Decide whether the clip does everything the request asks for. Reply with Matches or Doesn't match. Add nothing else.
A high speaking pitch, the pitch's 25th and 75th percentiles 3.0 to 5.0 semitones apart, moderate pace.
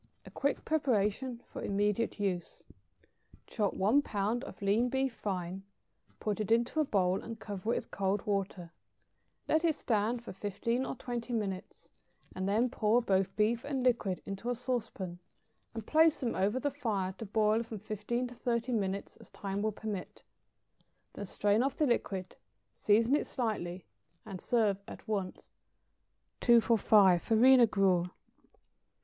Matches